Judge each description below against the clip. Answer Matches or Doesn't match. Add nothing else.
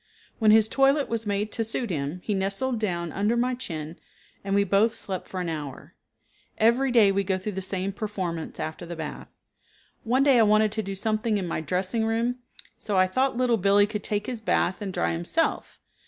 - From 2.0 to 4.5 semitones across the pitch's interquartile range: Matches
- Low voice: Doesn't match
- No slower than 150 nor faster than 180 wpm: Doesn't match